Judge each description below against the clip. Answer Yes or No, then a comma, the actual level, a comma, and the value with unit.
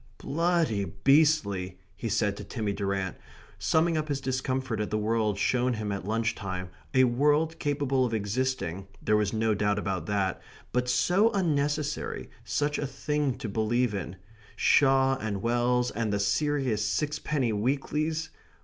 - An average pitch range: No, wide, 5.9 semitones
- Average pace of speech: Yes, average, 150 wpm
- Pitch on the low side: Yes, low, 120 Hz